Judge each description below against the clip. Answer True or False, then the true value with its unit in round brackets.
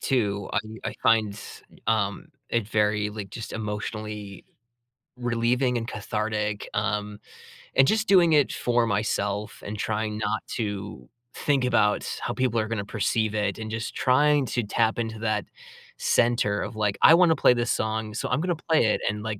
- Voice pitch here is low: True (110 Hz)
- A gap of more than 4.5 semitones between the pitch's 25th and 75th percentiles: False (2.5 semitones)